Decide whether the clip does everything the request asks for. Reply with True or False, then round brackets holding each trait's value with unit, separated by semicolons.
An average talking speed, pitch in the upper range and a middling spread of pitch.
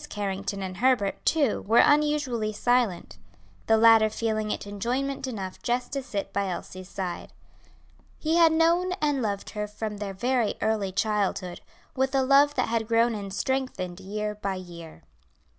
True (160 wpm; 220 Hz; 4.8 semitones)